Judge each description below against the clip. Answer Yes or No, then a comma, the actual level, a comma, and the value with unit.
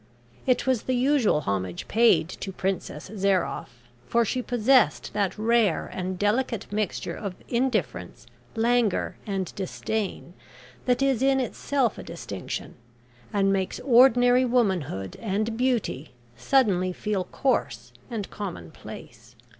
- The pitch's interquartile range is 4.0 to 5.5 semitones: Yes, average, 4.9 semitones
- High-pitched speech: Yes, high, 210 Hz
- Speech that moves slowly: Yes, slow, 120 wpm